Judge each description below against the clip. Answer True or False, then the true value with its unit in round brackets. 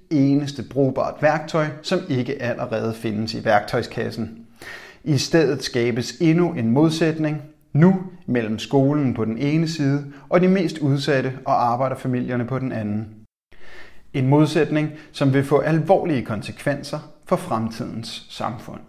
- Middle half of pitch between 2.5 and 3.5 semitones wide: False (4.4 semitones)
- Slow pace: True (130 wpm)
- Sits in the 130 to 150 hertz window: True (140 Hz)